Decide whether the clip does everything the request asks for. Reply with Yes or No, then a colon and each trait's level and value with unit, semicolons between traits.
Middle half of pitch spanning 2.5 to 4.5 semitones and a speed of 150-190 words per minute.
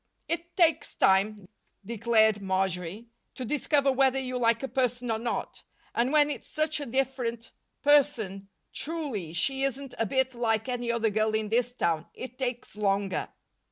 Yes: average, 3.9 semitones; average, 160 wpm